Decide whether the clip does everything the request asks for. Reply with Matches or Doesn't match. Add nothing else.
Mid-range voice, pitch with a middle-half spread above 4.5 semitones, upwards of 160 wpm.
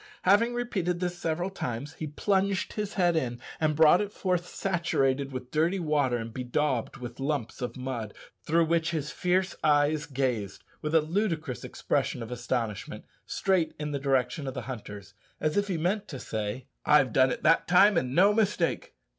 Matches